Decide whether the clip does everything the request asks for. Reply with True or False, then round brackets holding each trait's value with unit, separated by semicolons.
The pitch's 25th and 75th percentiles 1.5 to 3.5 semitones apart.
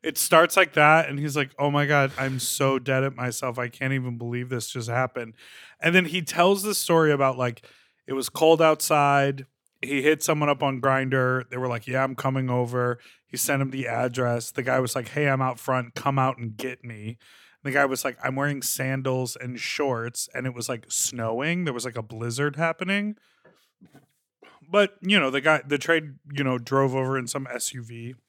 True (2.8 semitones)